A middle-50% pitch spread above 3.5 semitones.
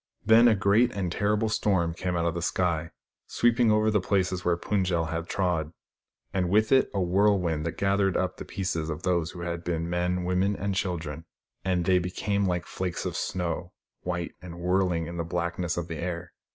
No: narrow, 2.4 semitones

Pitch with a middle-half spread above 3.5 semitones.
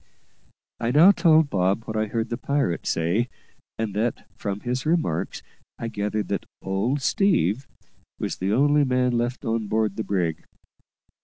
Yes: average, 4.8 semitones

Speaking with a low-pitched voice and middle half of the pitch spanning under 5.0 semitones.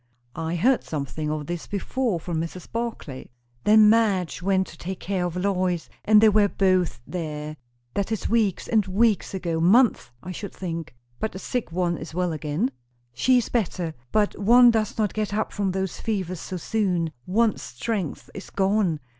No: high, 190 Hz; average, 4.2 semitones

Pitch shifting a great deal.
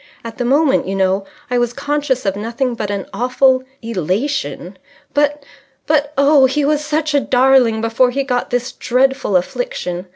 No: average, 4.1 semitones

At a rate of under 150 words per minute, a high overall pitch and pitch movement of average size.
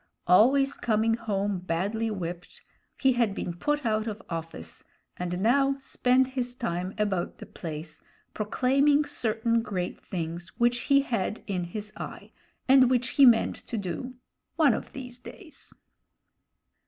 No: average, 140 wpm; high, 225 Hz; wide, 5.8 semitones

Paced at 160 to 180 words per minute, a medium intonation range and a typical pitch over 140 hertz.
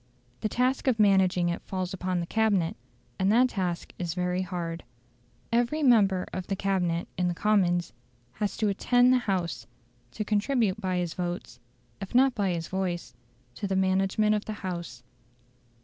Yes: average, 165 wpm; average, 3.2 semitones; high, 190 Hz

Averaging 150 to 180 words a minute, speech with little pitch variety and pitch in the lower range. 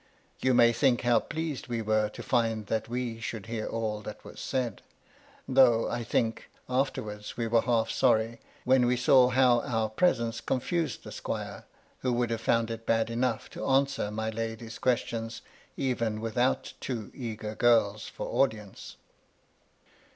Yes: average, 160 wpm; narrow, 2.1 semitones; low, 115 Hz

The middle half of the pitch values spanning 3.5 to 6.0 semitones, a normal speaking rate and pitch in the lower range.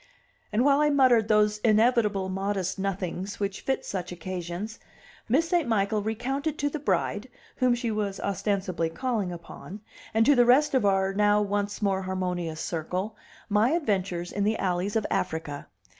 No: average, 3.9 semitones; average, 160 wpm; high, 205 Hz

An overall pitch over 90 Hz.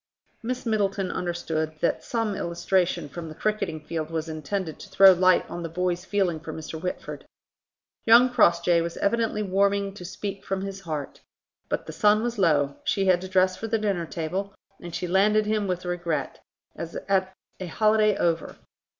Yes: medium, 185 Hz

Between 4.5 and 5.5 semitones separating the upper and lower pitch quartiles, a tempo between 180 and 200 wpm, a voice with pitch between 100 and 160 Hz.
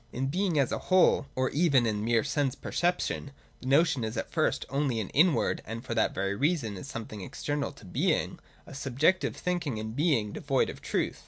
Yes: average, 4.8 semitones; average, 195 wpm; low, 135 Hz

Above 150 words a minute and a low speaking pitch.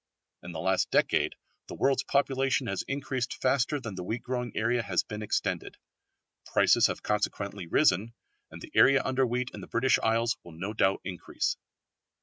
Yes: average, 170 wpm; low, 115 Hz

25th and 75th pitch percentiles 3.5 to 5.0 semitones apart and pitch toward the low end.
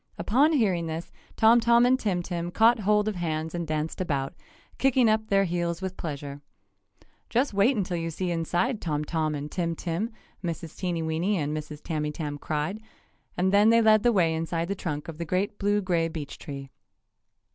No: average, 4.6 semitones; medium, 175 Hz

